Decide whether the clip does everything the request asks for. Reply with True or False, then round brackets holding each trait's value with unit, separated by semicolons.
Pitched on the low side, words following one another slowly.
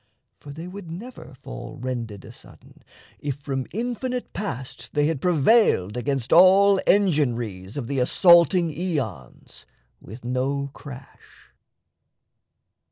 False (145 Hz; 110 wpm)